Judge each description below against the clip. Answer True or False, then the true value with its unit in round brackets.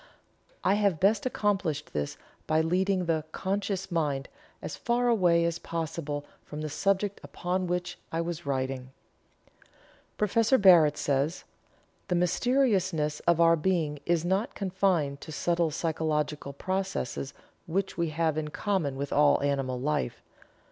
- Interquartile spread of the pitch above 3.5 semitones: True (4.1 semitones)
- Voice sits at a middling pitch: True (170 Hz)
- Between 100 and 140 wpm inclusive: True (135 wpm)